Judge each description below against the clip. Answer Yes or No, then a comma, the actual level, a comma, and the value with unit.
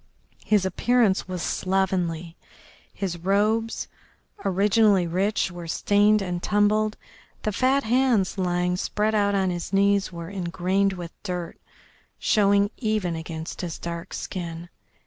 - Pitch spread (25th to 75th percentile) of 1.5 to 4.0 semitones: Yes, average, 2.9 semitones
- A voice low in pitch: No, high, 190 Hz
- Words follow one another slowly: Yes, slow, 125 wpm